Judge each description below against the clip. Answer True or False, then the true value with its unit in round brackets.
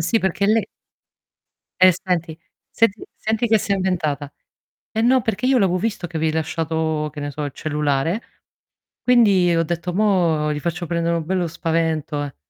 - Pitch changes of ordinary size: True (3.9 semitones)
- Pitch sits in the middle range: True (170 Hz)